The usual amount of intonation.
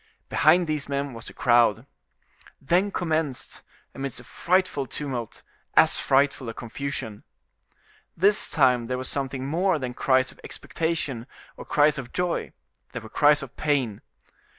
Yes: average, 3.8 semitones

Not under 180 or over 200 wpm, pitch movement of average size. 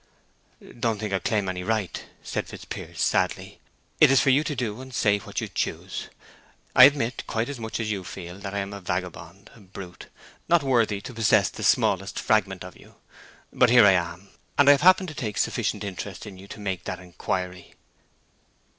Yes: average, 190 wpm; average, 4.2 semitones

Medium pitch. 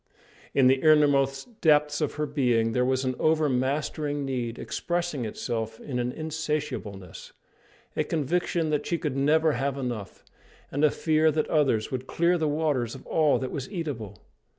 Yes: medium, 145 Hz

